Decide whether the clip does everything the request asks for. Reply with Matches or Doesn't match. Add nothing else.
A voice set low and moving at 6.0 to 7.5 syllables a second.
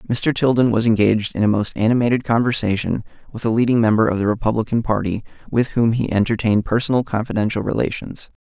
Matches